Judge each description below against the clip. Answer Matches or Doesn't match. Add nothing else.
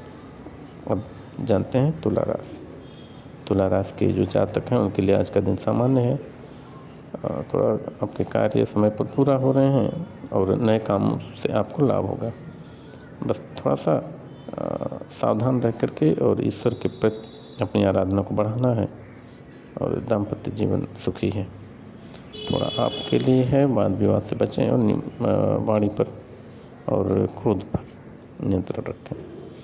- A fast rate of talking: Doesn't match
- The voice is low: Matches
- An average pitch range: Matches